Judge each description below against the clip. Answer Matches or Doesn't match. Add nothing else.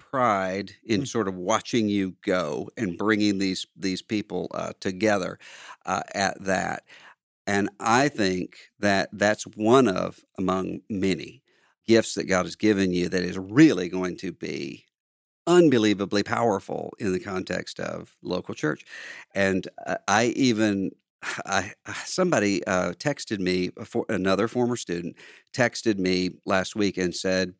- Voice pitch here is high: Doesn't match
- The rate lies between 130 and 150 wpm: Matches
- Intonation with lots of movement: Doesn't match